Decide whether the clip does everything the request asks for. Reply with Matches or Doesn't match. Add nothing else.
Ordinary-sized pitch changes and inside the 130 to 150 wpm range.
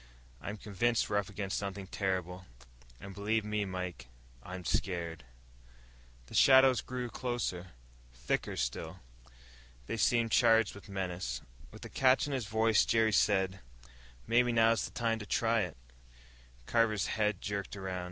Matches